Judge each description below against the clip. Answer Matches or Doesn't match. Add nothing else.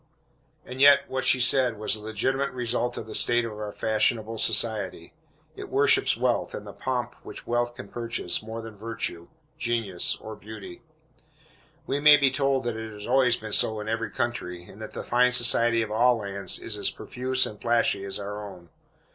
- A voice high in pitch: Doesn't match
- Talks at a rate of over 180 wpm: Matches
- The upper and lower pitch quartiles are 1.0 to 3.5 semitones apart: Matches